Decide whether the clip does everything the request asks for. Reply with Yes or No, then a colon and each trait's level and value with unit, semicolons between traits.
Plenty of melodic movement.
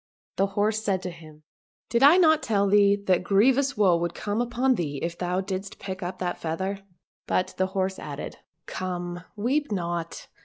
No: average, 3.4 semitones